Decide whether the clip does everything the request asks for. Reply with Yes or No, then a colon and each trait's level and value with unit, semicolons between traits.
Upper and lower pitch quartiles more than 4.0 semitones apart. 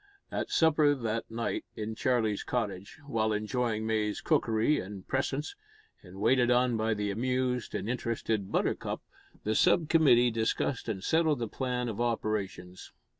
No: average, 2.9 semitones